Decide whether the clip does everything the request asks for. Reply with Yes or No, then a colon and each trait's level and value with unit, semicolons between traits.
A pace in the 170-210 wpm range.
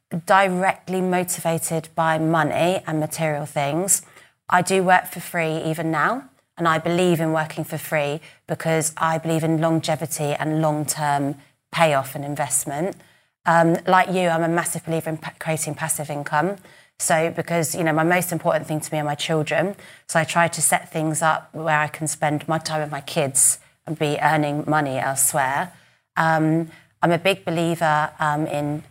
Yes: average, 175 wpm